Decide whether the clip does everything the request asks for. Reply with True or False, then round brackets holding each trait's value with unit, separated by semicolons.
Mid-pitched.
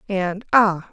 False (195 Hz)